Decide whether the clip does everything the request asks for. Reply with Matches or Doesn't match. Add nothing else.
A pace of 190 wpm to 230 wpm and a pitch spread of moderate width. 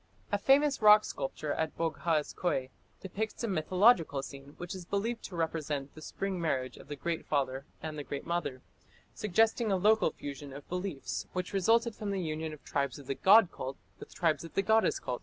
Doesn't match